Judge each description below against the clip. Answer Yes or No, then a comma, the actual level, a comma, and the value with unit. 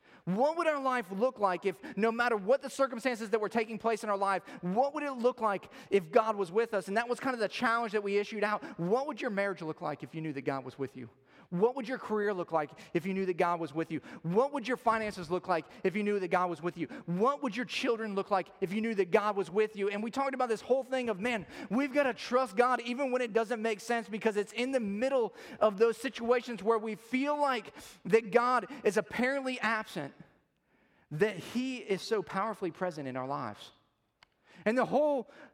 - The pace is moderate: No, fast, 245 wpm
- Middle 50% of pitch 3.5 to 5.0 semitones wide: Yes, average, 4.5 semitones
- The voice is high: Yes, high, 220 Hz